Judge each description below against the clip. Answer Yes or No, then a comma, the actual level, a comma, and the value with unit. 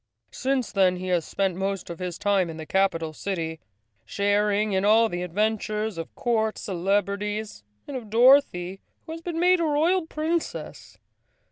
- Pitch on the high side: Yes, high, 205 Hz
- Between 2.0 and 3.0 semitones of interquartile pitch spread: No, average, 4.6 semitones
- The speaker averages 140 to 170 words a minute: Yes, average, 160 wpm